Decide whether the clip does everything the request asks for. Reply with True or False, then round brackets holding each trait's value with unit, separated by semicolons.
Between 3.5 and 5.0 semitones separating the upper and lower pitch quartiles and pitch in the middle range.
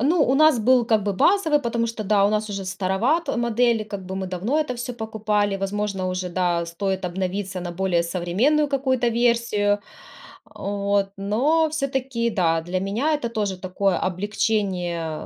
False (4.3 semitones; 205 Hz)